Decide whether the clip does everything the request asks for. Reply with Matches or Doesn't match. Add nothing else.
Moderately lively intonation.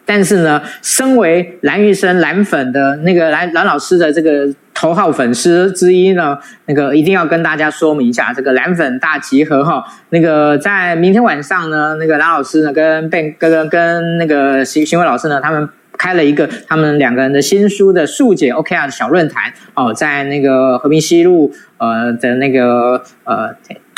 Matches